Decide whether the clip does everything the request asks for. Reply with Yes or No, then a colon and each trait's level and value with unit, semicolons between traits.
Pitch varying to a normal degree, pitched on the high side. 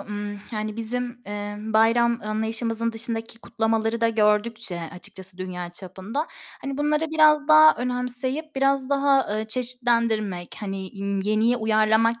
Yes: average, 3.0 semitones; high, 225 Hz